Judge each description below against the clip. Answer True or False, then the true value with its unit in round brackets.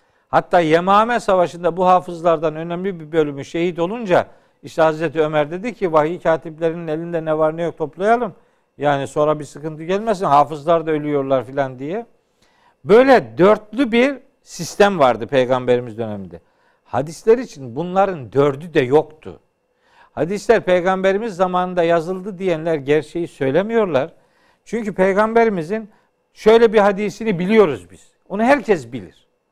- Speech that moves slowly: False (130 wpm)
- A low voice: False (170 Hz)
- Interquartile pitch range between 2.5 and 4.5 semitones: False (5.6 semitones)